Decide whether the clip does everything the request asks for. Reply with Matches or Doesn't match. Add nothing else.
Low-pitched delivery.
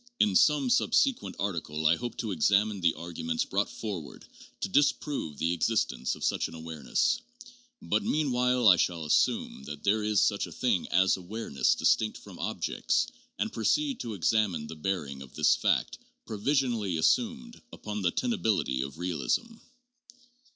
Matches